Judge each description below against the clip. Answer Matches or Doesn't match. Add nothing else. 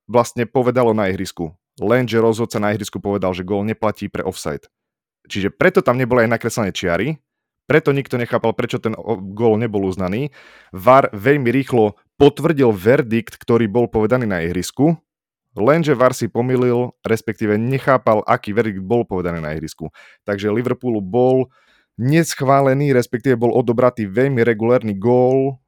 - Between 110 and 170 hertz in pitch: Matches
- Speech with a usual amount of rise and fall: Matches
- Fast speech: Doesn't match